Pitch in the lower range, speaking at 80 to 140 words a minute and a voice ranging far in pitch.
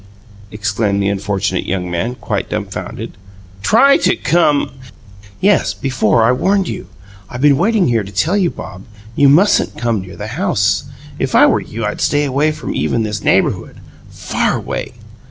No: low, 120 Hz; average, 170 wpm; wide, 7.2 semitones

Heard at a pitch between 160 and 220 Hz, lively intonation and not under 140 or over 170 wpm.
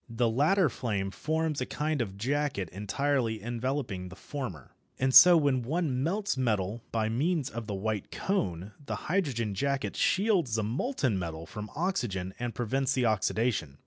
No: low, 120 Hz; wide, 5.8 semitones; average, 160 wpm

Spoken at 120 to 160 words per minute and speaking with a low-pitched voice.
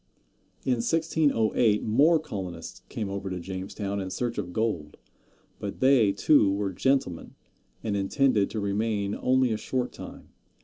Yes: average, 140 wpm; low, 105 Hz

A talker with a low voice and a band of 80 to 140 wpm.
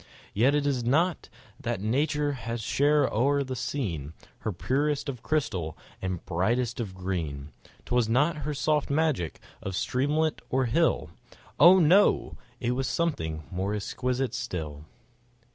Yes: low, 125 Hz; slow, 135 wpm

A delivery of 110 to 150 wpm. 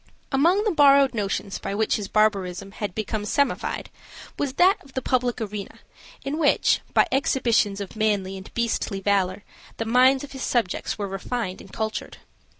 No: average, 165 wpm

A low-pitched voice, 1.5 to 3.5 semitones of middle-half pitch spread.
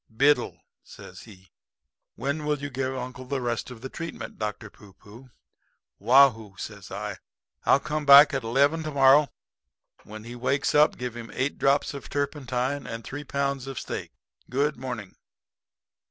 Yes: low, 130 Hz; average, 3.1 semitones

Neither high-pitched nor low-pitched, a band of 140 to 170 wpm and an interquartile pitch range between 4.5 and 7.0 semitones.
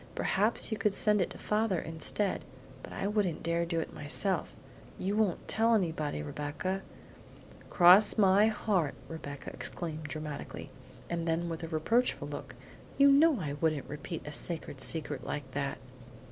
Yes: medium, 170 Hz; average, 160 wpm; average, 5.1 semitones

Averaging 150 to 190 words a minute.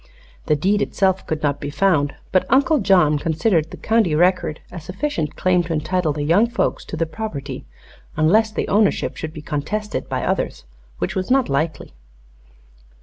Yes: average, 170 wpm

